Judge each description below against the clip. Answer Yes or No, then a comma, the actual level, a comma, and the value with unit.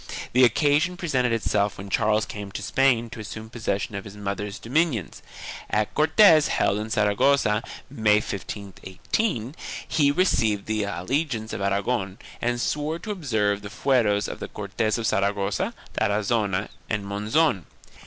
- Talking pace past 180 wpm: No, average, 145 wpm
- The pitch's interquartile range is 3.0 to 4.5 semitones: No, average, 4.9 semitones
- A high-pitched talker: No, low, 110 Hz